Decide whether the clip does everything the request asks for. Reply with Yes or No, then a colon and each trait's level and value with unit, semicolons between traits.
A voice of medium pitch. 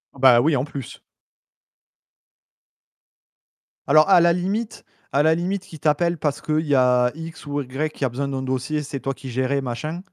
Yes: medium, 145 Hz